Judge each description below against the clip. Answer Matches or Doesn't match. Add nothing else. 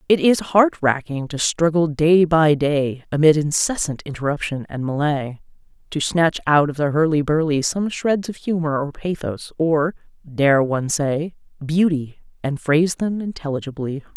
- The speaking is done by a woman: Matches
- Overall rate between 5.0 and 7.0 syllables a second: Doesn't match